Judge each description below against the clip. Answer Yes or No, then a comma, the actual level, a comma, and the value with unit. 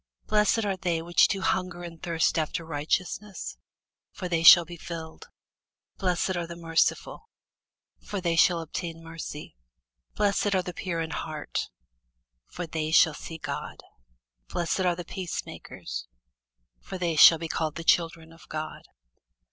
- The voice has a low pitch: No, medium, 170 Hz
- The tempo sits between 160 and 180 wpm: No, average, 150 wpm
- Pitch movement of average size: No, narrow, 2.0 semitones